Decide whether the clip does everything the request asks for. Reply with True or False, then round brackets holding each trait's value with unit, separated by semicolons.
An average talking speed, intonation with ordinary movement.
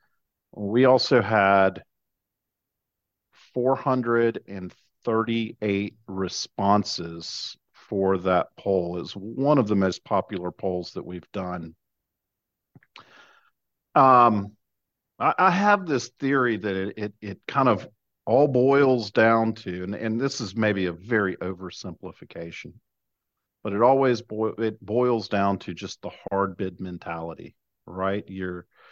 False (120 wpm; 3.8 semitones)